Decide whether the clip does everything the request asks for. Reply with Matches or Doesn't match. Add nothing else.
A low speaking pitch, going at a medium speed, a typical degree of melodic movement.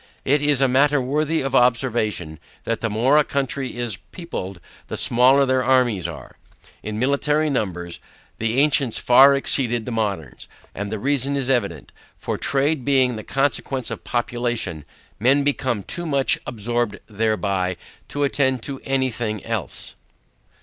Matches